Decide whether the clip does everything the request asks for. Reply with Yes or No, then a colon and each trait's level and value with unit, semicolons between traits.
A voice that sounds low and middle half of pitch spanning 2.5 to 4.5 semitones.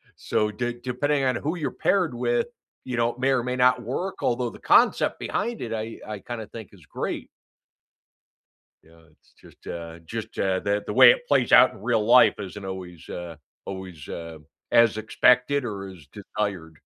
No: low, 110 Hz; average, 4.9 semitones